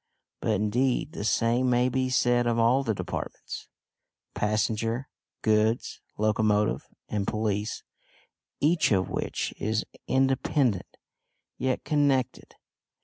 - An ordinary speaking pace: No, slow, 105 wpm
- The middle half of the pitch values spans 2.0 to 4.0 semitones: Yes, average, 3.2 semitones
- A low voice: Yes, low, 115 Hz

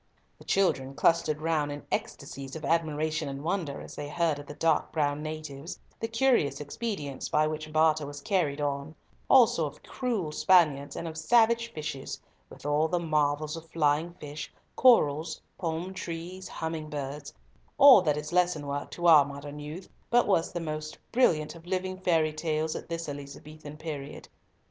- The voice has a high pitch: No, medium, 155 Hz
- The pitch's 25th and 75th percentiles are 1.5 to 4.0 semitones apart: Yes, average, 2.7 semitones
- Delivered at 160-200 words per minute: Yes, average, 165 wpm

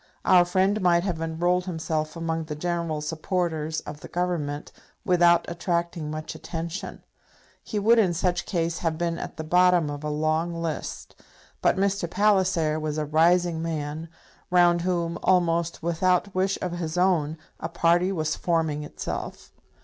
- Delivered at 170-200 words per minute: No, average, 155 wpm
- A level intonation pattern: Yes, narrow, 2.2 semitones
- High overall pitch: No, medium, 170 Hz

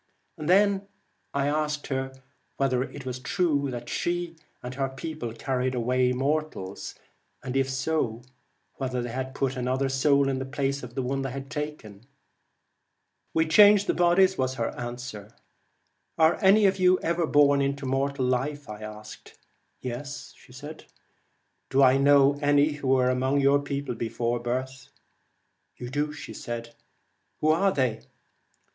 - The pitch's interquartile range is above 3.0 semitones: No, average, 2.7 semitones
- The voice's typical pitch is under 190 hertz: Yes, low, 135 Hz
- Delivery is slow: No, average, 145 wpm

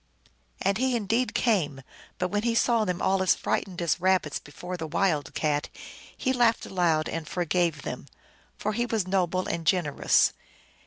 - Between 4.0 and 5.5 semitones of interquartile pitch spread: Yes, average, 4.4 semitones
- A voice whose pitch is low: No, medium, 185 Hz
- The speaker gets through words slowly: No, average, 170 wpm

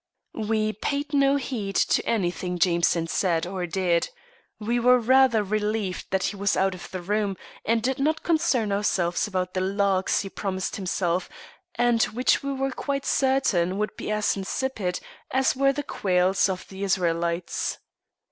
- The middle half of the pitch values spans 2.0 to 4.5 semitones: No, average, 5.0 semitones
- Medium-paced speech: Yes, average, 160 wpm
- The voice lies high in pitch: Yes, high, 200 Hz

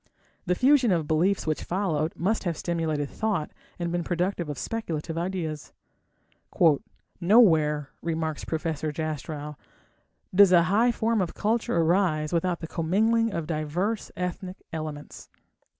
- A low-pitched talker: No, medium, 170 Hz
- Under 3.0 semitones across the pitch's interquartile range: No, average, 3.9 semitones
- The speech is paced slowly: Yes, slow, 130 wpm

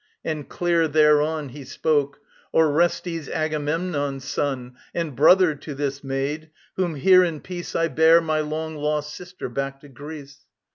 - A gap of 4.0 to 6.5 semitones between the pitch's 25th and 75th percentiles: No, narrow, 2.4 semitones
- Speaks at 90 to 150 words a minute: Yes, average, 145 wpm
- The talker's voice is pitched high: No, medium, 150 Hz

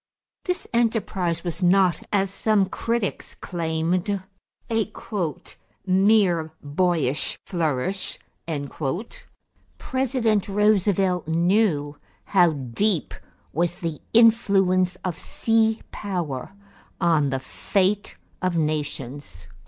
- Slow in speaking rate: Yes, slow, 85 wpm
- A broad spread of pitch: No, average, 4.3 semitones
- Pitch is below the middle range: No, medium, 185 Hz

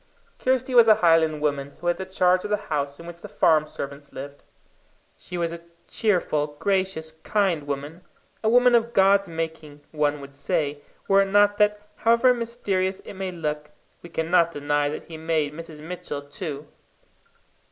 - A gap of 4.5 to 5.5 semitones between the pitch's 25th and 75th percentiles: Yes, average, 4.9 semitones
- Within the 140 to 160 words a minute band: No, average, 175 wpm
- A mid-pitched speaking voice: Yes, medium, 165 Hz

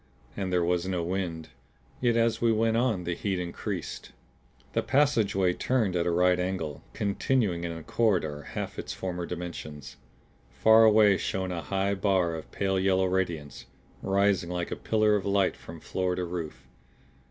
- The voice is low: Yes, very low, 95 Hz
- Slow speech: No, average, 165 wpm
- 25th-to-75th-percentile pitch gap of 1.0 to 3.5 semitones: Yes, average, 2.9 semitones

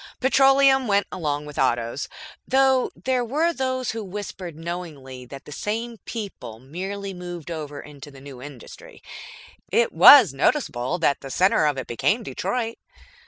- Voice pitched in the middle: Yes, medium, 180 Hz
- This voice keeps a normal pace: Yes, average, 150 wpm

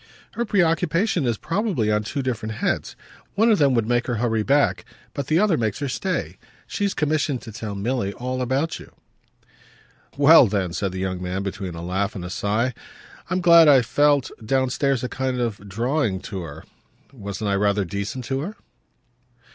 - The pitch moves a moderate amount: No, wide, 6.3 semitones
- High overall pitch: No, low, 125 Hz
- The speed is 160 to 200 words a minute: Yes, average, 180 wpm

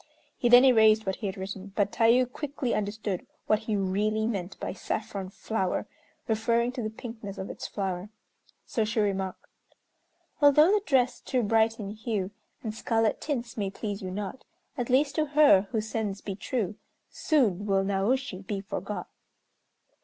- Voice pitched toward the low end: No, high, 215 Hz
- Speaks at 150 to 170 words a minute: Yes, average, 165 wpm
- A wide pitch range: No, average, 3.4 semitones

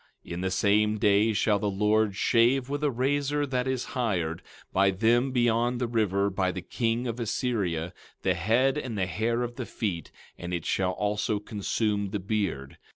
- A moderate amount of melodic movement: Yes, average, 3.8 semitones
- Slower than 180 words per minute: No, average, 185 wpm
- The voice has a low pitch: Yes, low, 110 Hz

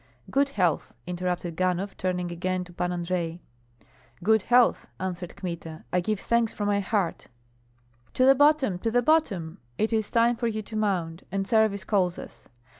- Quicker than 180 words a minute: No, average, 170 wpm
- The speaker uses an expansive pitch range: No, average, 3.9 semitones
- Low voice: No, high, 190 Hz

